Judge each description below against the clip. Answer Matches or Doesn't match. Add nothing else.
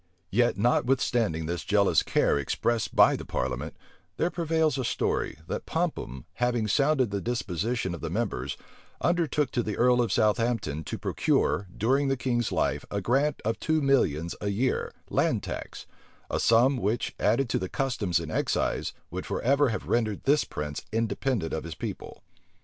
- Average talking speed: Matches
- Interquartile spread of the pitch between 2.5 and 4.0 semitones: Doesn't match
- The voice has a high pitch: Doesn't match